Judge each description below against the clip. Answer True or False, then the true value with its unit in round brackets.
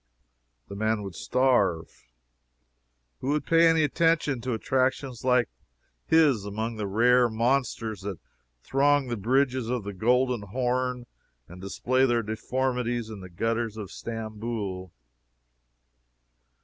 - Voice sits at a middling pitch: False (120 Hz)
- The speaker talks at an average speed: False (125 wpm)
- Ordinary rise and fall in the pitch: True (3.3 semitones)